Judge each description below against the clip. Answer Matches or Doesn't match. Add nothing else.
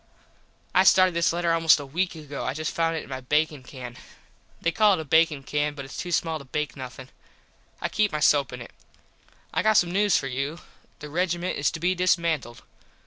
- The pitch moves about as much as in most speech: Matches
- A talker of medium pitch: Matches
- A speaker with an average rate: Doesn't match